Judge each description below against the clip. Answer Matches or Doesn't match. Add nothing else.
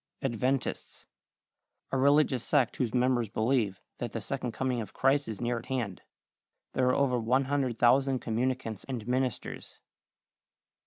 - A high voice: Doesn't match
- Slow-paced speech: Matches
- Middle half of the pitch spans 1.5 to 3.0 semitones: Matches